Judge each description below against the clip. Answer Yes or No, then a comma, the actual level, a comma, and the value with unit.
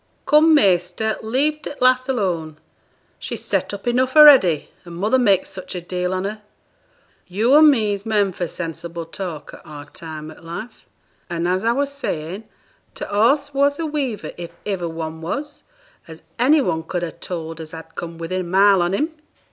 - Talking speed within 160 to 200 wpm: Yes, average, 180 wpm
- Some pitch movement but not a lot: No, wide, 7.1 semitones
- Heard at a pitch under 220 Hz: Yes, high, 190 Hz